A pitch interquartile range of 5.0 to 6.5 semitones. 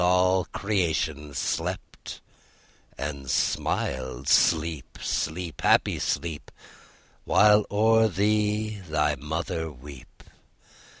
Yes: wide, 5.6 semitones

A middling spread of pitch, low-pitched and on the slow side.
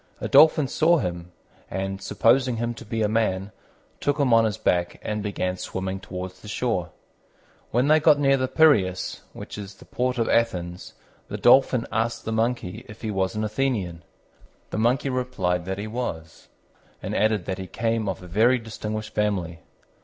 No: average, 4.6 semitones; low, 110 Hz; average, 180 wpm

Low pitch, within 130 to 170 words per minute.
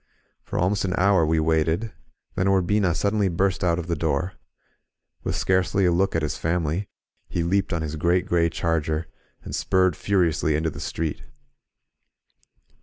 Yes: very low, 85 Hz; average, 165 wpm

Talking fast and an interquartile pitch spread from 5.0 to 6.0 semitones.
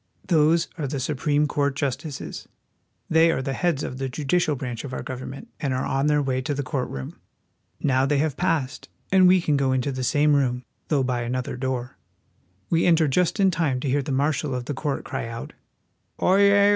No: fast, 210 wpm; average, 3.3 semitones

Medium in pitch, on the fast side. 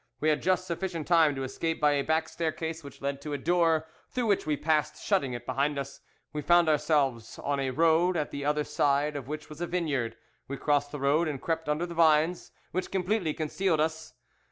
Yes: medium, 155 Hz; fast, 215 wpm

